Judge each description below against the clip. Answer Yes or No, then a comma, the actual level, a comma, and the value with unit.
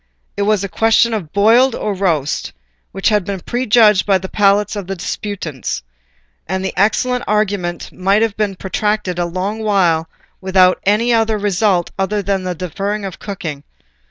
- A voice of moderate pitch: No, high, 200 Hz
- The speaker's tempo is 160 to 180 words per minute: Yes, average, 165 wpm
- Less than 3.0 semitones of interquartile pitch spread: Yes, narrow, 2.4 semitones